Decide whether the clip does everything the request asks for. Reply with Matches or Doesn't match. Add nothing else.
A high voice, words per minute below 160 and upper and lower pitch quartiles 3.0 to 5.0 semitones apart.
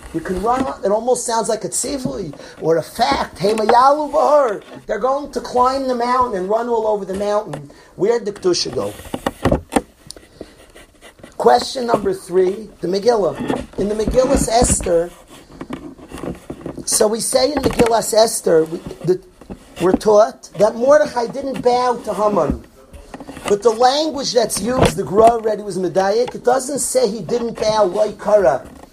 Matches